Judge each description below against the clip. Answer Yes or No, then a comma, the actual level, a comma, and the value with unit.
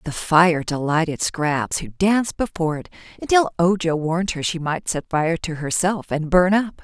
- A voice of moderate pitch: Yes, medium, 170 Hz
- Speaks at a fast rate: No, average, 185 wpm